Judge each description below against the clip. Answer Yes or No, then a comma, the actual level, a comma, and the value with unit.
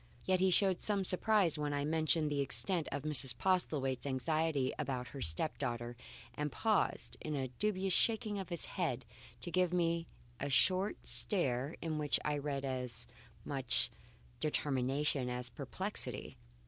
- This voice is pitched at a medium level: Yes, medium, 150 Hz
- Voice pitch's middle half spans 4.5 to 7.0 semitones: Yes, wide, 5.4 semitones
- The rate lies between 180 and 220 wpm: No, average, 150 wpm